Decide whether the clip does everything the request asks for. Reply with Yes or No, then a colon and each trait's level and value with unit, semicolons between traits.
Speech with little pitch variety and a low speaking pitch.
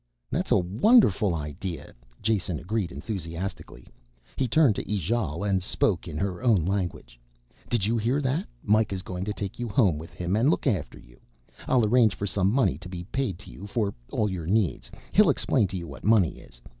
No: average, 4.2 semitones; low, 100 Hz